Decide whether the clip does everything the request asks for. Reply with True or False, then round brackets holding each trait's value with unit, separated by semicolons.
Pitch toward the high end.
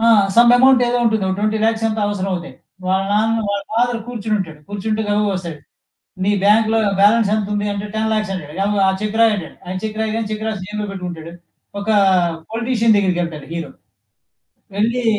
True (210 Hz)